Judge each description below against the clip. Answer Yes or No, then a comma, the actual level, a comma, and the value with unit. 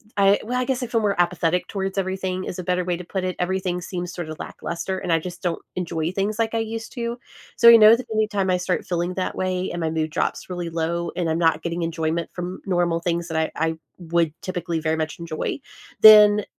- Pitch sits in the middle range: Yes, medium, 180 Hz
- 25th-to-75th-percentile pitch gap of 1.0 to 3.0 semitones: Yes, narrow, 2.6 semitones